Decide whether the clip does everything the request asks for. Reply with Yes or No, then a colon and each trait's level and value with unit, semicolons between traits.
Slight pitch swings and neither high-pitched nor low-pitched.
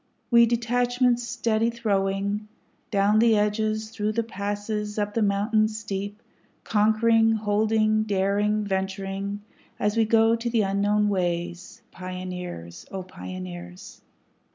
No: narrow, 2.3 semitones; high, 210 Hz